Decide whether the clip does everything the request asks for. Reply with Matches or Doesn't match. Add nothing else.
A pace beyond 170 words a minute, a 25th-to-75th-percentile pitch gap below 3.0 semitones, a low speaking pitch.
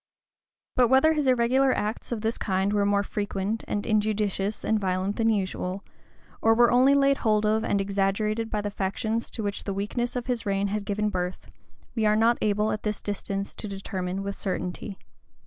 Doesn't match